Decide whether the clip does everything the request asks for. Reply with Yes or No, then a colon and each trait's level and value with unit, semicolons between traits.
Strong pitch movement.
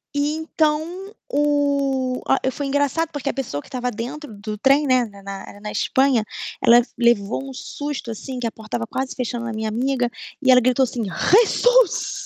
No: average, 3.8 semitones